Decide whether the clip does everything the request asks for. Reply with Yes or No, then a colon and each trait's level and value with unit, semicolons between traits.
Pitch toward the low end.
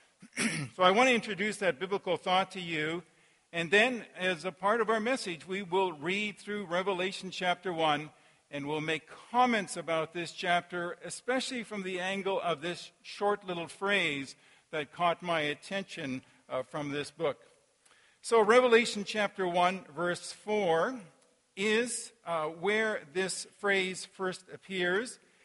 No: medium, 185 Hz